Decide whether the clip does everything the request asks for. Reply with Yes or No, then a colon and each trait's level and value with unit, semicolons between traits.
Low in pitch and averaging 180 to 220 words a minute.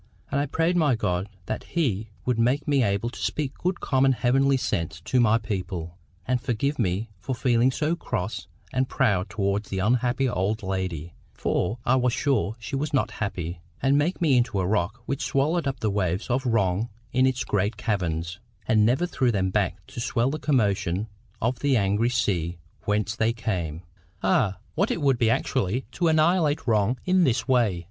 Yes: low, 115 Hz; average, 185 wpm